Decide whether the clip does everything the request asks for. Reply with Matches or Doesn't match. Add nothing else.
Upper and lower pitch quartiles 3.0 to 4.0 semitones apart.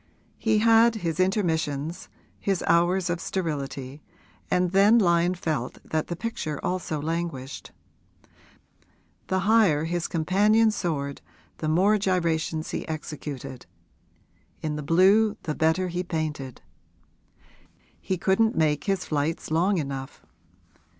Matches